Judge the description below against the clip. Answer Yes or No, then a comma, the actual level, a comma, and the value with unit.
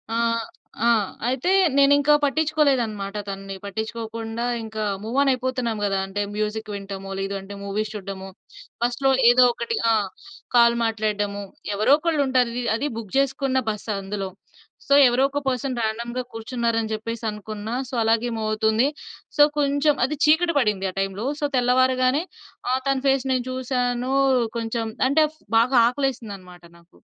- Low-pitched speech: No, high, 235 Hz